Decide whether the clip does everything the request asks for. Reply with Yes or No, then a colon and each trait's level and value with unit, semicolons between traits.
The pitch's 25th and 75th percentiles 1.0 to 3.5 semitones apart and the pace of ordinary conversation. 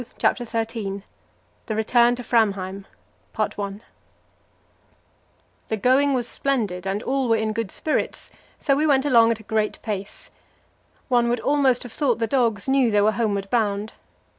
Yes: average, 3.2 semitones; average, 150 wpm